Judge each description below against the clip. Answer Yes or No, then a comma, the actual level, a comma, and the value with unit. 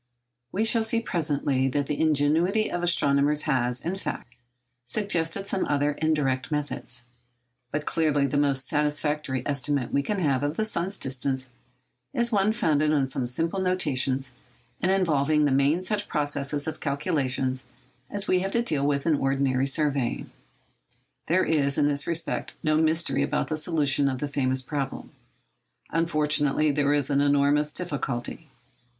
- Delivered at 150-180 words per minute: Yes, average, 155 wpm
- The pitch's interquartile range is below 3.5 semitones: Yes, average, 3.0 semitones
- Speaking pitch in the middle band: Yes, medium, 145 Hz